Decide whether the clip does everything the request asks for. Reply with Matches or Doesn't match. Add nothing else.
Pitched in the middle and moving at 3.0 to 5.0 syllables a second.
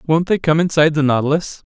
Doesn't match